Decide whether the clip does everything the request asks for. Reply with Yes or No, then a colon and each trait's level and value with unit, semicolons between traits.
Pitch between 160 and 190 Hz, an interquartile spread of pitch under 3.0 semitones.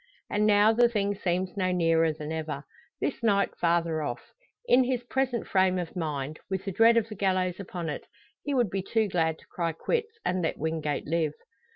No: medium, 185 Hz; average, 4.8 semitones